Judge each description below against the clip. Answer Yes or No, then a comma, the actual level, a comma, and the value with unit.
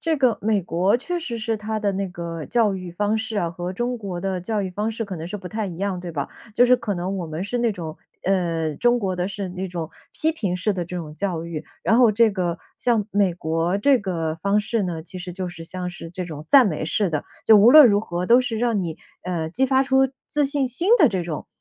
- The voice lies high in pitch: Yes, high, 195 Hz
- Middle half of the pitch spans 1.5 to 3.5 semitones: No, average, 4.5 semitones